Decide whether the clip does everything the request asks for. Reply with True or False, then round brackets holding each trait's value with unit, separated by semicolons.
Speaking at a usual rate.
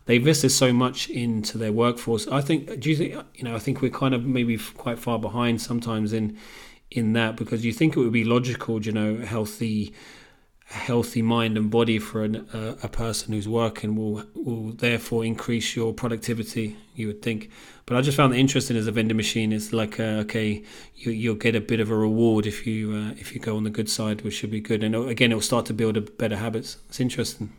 False (230 wpm)